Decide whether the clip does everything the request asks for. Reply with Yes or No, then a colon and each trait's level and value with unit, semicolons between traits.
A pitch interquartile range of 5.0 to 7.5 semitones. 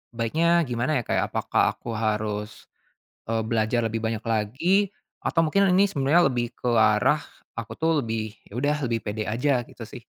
Yes: average, 5.3 semitones